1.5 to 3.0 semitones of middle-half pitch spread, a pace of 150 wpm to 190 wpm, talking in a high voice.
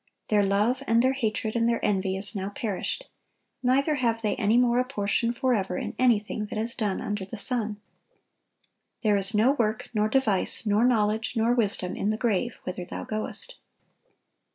Yes: narrow, 2.6 semitones; average, 175 wpm; high, 220 Hz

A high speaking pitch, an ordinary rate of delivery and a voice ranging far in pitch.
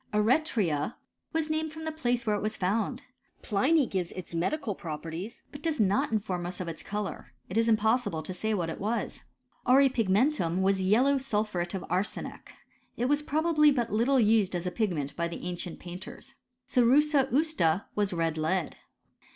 Yes: high, 215 Hz; average, 170 wpm; wide, 6.9 semitones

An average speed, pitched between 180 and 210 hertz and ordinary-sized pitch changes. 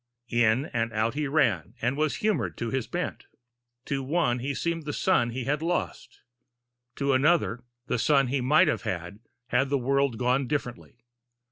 No: average, 170 wpm; low, 135 Hz; average, 3.6 semitones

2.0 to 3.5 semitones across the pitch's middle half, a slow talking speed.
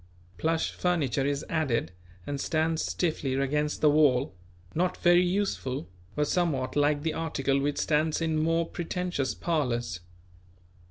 Yes: average, 3.1 semitones; slow, 130 wpm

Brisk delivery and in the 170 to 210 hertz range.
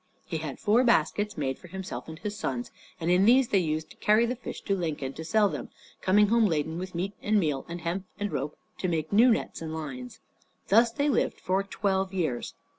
Yes: fast, 220 wpm; medium, 185 Hz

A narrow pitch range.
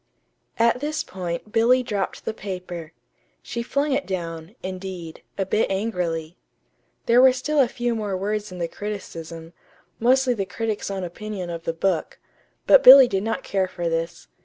No: average, 5.0 semitones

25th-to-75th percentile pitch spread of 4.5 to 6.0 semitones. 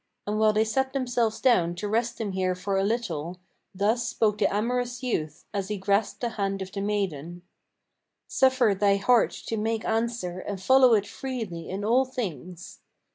No: average, 3.7 semitones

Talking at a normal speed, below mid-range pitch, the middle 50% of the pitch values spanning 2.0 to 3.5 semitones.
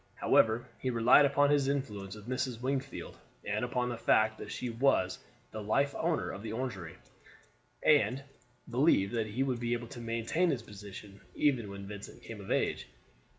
No: average, 175 wpm; low, 120 Hz; average, 4.1 semitones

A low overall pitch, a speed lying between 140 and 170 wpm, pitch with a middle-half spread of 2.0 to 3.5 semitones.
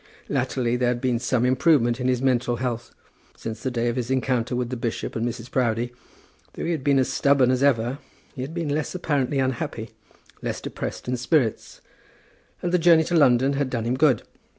No: low, 125 Hz; average, 200 wpm; narrow, 2.6 semitones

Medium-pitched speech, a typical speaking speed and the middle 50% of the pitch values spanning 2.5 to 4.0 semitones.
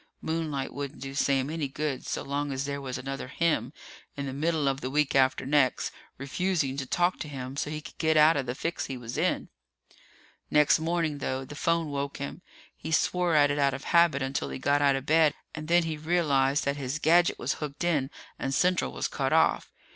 No: medium, 145 Hz; fast, 215 wpm; average, 2.8 semitones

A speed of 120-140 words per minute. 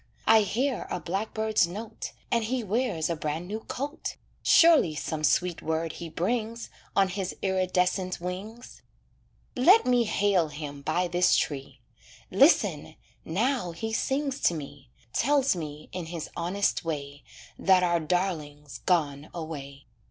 Yes: slow, 135 wpm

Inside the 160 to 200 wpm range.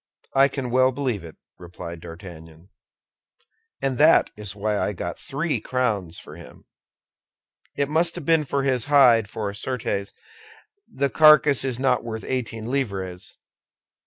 No: average, 140 wpm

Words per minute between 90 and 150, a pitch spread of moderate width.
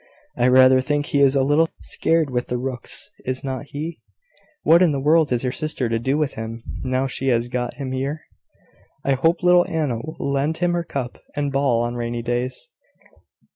No: average, 200 wpm; average, 3.5 semitones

